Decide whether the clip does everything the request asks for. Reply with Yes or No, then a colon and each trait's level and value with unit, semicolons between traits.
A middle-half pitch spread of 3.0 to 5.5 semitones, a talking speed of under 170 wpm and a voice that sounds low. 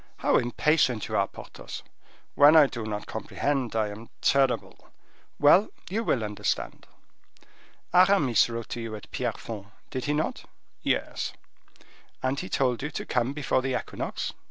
Yes: average, 4.3 semitones; average, 150 wpm; low, 130 Hz